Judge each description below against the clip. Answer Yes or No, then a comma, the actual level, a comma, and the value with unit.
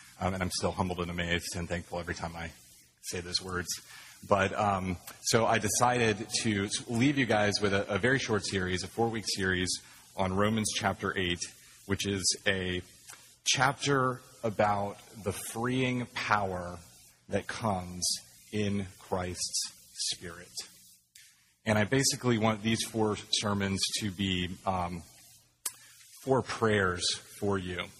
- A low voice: Yes, low, 100 Hz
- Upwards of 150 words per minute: No, average, 140 wpm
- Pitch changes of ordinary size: Yes, average, 3.8 semitones